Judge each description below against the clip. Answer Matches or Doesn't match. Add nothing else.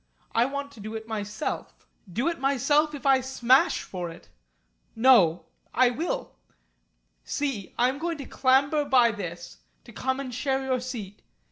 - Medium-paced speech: Matches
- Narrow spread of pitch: Doesn't match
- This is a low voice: Doesn't match